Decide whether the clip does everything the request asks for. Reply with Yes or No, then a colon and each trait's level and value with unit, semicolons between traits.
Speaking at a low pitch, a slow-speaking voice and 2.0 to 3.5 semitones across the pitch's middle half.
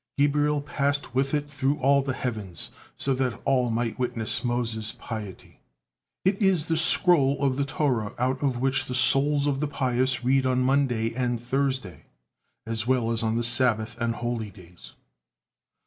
No: low, 130 Hz; average, 165 wpm; average, 3.2 semitones